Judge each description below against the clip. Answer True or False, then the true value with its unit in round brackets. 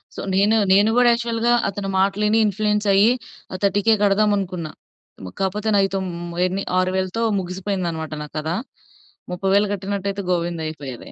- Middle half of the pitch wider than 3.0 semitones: False (2.4 semitones)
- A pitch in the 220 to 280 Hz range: False (195 Hz)